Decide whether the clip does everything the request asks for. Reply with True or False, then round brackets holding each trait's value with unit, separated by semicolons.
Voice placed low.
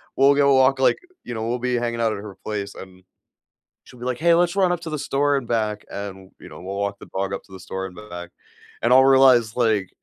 True (115 Hz)